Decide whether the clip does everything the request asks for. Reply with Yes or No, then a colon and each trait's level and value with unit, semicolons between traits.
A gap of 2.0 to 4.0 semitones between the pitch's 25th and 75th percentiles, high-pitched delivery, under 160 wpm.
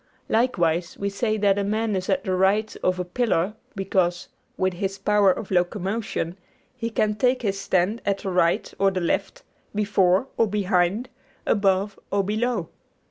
No: narrow, 2.5 semitones; high, 195 Hz; average, 165 wpm